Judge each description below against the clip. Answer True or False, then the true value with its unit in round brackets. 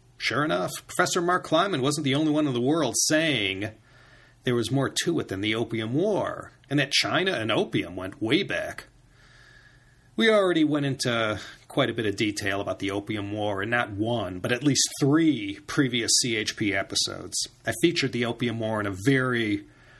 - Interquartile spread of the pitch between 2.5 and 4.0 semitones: False (5.4 semitones)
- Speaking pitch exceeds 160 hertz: False (120 Hz)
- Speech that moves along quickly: False (185 wpm)